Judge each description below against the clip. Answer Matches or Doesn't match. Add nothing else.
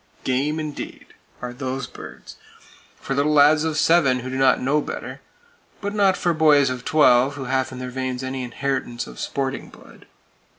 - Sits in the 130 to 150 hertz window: Matches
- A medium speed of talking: Matches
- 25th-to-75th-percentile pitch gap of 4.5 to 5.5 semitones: Doesn't match